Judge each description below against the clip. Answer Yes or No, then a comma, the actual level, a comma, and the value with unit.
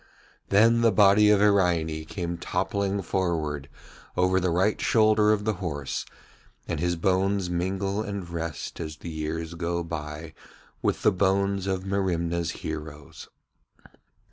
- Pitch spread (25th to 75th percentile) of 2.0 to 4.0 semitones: Yes, average, 3.3 semitones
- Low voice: Yes, very low, 90 Hz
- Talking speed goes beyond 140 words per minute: No, slow, 135 wpm